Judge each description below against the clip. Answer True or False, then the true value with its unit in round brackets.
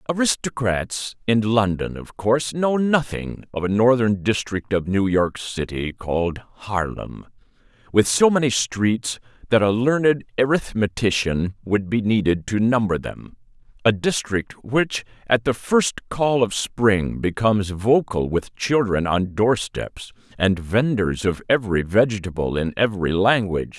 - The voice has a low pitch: True (110 Hz)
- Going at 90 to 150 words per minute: True (140 wpm)